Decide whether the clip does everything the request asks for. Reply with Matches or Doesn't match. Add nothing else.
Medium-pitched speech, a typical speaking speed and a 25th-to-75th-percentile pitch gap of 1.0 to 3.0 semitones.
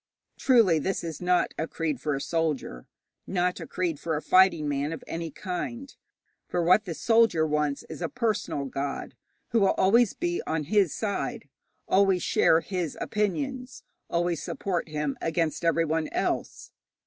Doesn't match